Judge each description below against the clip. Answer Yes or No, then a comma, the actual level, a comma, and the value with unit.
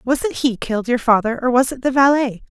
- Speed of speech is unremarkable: No, fast, 255 wpm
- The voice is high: Yes, very high, 250 Hz